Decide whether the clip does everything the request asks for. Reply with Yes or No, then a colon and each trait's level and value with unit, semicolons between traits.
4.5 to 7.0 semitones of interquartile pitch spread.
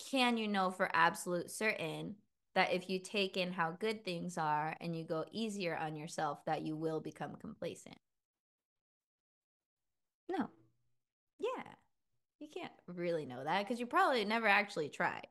Yes: average, 5.1 semitones